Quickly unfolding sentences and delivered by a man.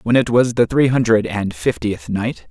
Yes: fast, 215 wpm; male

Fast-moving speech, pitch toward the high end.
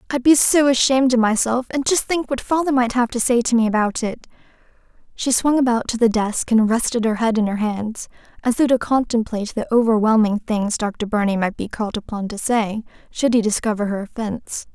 Yes: fast, 210 wpm; high, 230 Hz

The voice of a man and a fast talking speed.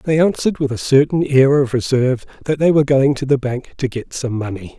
Yes: male; fast, 240 wpm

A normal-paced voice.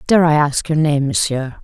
No: fast, 220 wpm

